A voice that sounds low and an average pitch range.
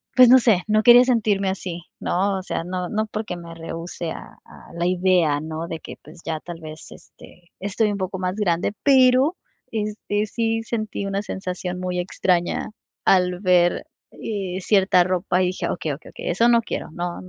No: medium, 185 Hz; average, 3.4 semitones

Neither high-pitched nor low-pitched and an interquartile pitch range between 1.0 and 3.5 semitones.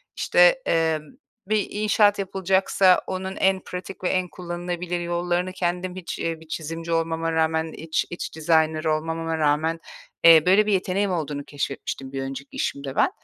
Yes: medium, 170 Hz; average, 2.7 semitones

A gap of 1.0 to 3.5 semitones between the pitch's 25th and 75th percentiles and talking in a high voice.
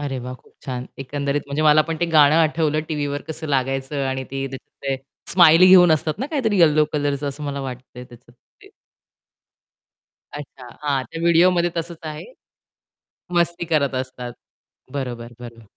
No: average, 3.2 semitones; medium, 145 Hz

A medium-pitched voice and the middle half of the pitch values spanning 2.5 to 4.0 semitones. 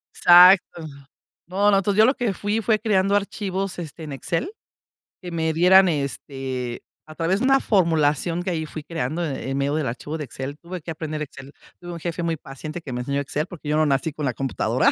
No: medium, 165 Hz; average, 4.6 semitones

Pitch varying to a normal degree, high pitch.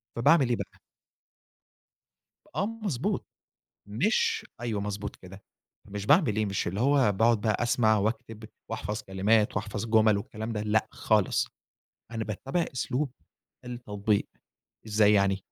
No: average, 3.0 semitones; low, 110 Hz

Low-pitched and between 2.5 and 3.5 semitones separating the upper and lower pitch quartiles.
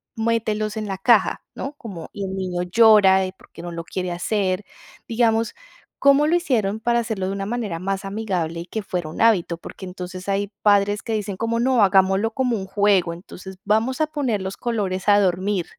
No: high, 205 Hz; average, 3.2 semitones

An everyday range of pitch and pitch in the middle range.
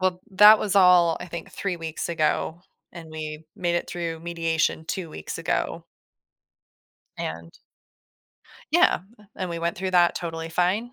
No: narrow, 2.0 semitones; medium, 170 Hz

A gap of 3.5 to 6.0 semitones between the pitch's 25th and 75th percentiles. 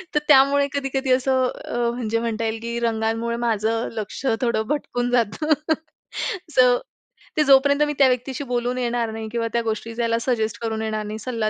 No: average, 2.7 semitones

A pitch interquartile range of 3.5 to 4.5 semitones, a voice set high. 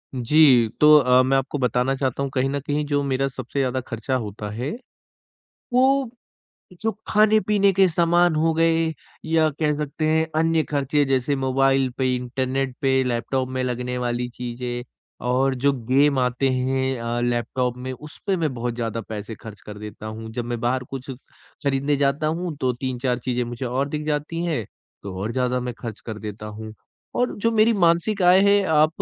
No: average, 3.8 semitones; low, 130 Hz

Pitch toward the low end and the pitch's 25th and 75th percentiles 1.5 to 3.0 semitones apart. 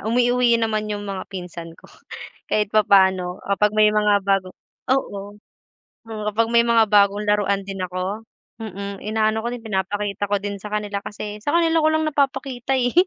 No: high, 210 Hz; narrow, 2.6 semitones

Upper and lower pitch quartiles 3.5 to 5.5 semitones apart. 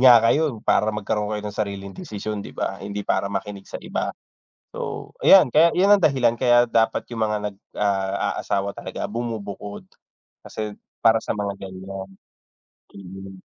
No: average, 2.8 semitones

